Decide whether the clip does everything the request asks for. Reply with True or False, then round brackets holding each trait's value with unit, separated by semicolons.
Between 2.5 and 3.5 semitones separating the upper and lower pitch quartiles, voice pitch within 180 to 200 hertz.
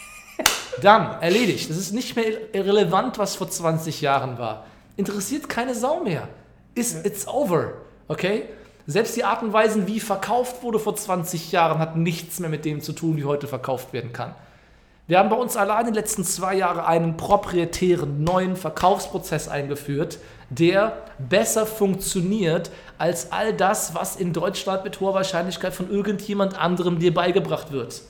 False (4.1 semitones; 185 Hz)